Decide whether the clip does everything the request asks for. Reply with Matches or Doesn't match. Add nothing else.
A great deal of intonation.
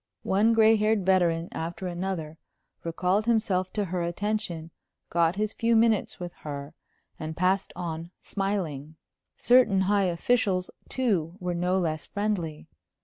Doesn't match